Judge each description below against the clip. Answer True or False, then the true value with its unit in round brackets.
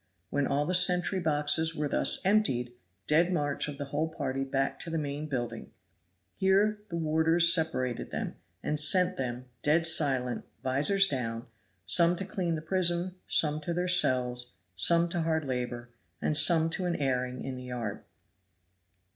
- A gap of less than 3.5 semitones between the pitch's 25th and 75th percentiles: False (4.8 semitones)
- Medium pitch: True (155 Hz)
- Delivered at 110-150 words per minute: False (165 wpm)